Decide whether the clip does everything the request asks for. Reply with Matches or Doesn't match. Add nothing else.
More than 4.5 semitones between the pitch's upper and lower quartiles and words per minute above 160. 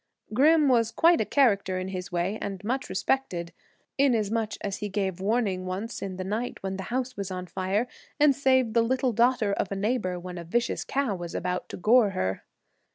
Matches